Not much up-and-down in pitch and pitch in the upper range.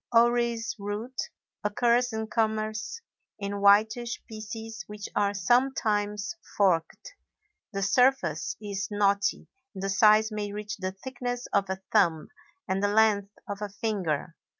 Yes: narrow, 2.1 semitones; high, 210 Hz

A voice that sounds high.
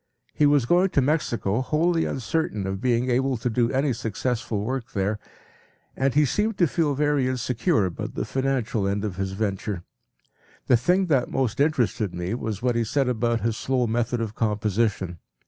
No: low, 120 Hz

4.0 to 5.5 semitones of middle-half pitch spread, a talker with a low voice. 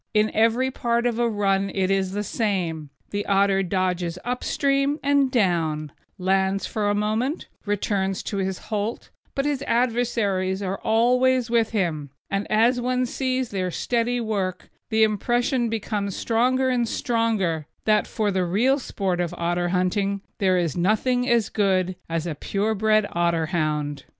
No: average, 4.3 semitones; high, 205 Hz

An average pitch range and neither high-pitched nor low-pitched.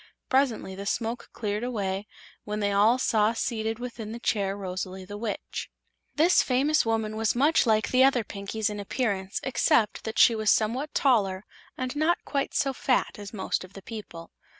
No: average, 3.6 semitones; high, 220 Hz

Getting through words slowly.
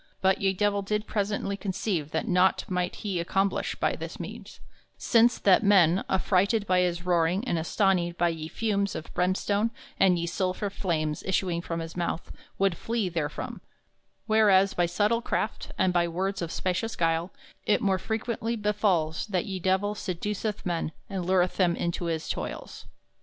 No: average, 165 wpm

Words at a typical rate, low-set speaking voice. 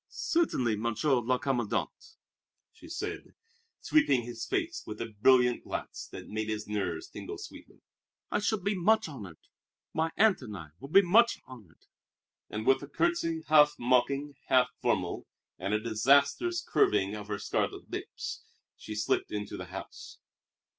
Yes: average, 155 wpm; low, 125 Hz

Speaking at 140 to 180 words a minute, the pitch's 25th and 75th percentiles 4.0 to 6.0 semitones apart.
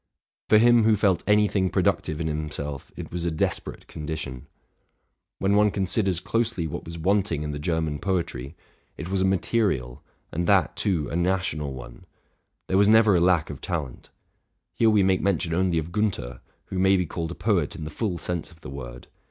No: average, 195 wpm; average, 4.4 semitones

